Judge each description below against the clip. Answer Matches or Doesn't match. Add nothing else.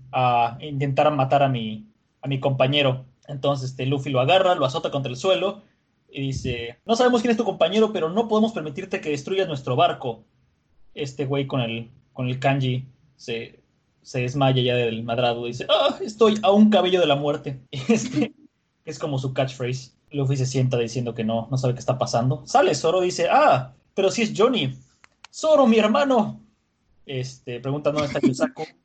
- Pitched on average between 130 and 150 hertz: Matches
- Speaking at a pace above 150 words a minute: Matches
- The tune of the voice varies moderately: Doesn't match